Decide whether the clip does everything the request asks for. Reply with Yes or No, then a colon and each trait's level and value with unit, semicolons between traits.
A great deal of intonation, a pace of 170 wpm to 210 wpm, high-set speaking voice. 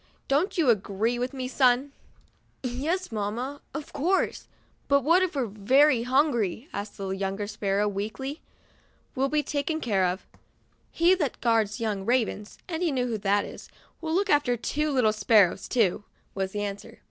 Yes: wide, 5.7 semitones; average, 180 wpm; high, 245 Hz